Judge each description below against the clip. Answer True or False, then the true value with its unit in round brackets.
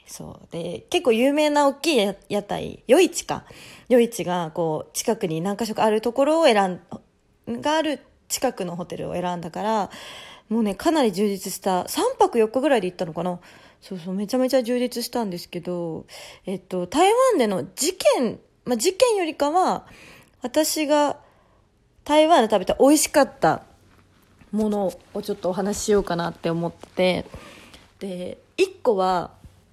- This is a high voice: True (220 Hz)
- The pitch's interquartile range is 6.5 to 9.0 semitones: True (7.9 semitones)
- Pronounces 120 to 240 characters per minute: False (295 characters per minute)